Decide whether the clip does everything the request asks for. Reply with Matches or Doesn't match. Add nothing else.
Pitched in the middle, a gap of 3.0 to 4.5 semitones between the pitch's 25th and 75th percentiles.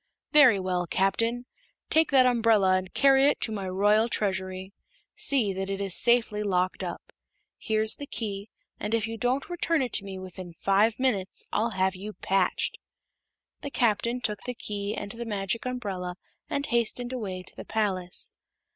Doesn't match